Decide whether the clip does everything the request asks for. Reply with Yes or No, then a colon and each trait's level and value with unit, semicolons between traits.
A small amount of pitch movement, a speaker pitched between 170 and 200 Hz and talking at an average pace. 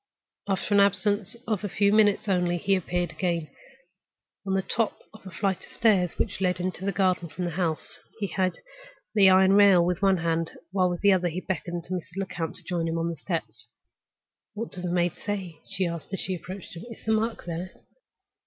No: narrow, 2.3 semitones; medium, 185 Hz; fast, 215 wpm